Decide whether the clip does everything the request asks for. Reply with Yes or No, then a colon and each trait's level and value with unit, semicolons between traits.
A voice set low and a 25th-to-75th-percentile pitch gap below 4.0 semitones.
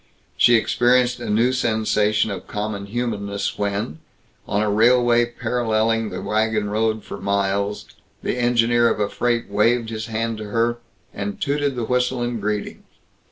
Yes: low, 110 Hz; narrow, 2.5 semitones